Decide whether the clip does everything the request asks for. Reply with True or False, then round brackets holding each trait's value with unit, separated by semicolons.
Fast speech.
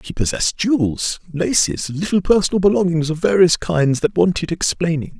False (150 wpm)